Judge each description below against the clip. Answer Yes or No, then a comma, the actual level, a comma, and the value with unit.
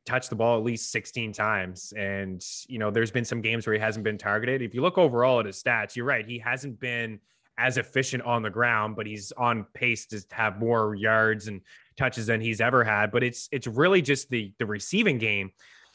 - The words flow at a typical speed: No, fast, 220 wpm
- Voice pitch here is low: Yes, low, 115 Hz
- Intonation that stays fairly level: Yes, narrow, 2.3 semitones